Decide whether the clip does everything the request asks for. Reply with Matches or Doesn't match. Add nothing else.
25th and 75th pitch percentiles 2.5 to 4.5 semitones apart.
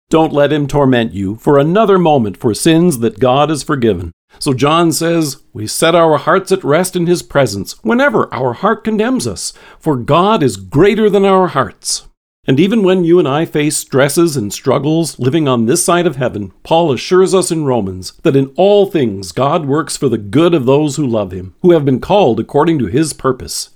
Doesn't match